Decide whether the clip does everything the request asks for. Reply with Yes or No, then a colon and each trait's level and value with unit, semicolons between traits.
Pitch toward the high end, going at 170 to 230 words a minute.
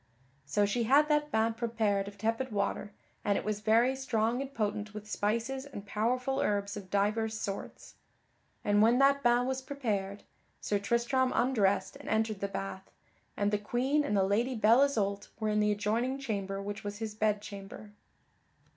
Yes: high, 215 Hz; average, 175 wpm